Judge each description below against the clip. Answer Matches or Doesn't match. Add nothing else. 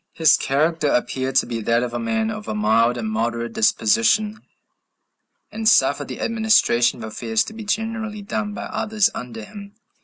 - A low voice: Doesn't match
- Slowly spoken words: Doesn't match